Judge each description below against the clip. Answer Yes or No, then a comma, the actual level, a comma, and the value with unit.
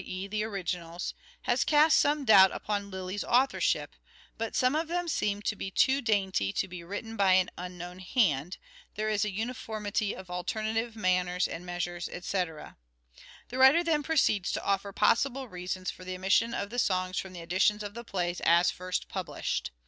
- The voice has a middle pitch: No, high, 200 Hz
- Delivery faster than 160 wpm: Yes, average, 170 wpm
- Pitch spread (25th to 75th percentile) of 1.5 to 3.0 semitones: No, average, 3.7 semitones